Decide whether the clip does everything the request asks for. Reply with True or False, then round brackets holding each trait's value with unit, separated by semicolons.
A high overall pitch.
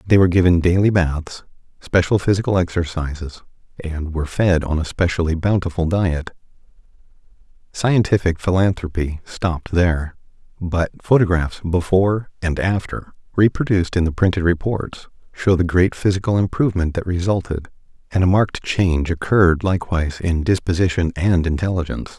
False (90 Hz)